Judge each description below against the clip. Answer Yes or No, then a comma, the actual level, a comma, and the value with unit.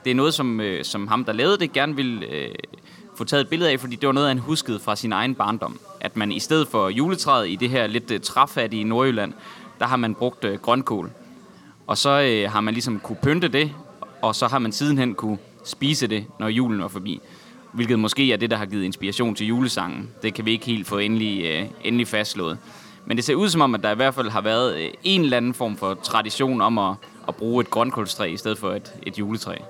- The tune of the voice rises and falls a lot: No, average, 3.7 semitones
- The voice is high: No, low, 115 Hz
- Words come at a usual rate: No, fast, 230 wpm